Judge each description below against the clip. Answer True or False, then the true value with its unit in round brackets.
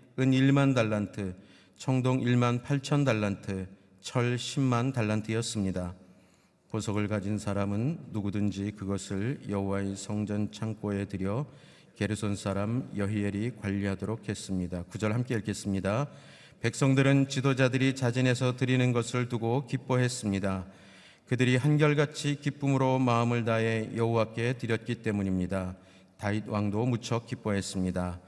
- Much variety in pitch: False (4.4 semitones)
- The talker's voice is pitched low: True (110 Hz)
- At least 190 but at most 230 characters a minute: False (295 characters per minute)